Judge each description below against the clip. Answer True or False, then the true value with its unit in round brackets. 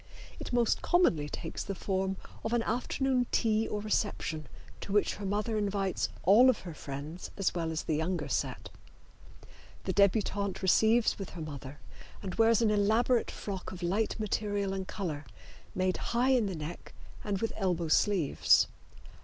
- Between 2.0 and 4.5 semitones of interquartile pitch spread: True (3.9 semitones)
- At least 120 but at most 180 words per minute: True (160 wpm)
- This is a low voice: False (200 Hz)